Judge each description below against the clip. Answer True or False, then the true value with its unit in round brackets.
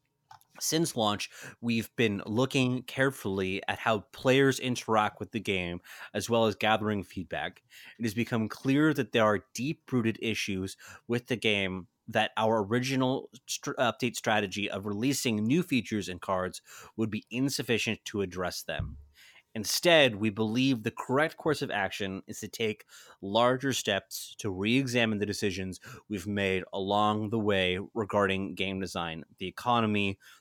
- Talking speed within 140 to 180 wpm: True (150 wpm)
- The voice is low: True (110 Hz)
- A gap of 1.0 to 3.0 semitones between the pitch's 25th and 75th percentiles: False (3.4 semitones)